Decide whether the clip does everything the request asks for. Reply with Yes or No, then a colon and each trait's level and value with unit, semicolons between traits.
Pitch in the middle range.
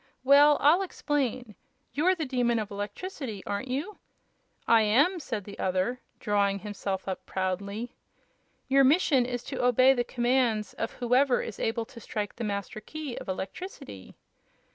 No: high, 240 Hz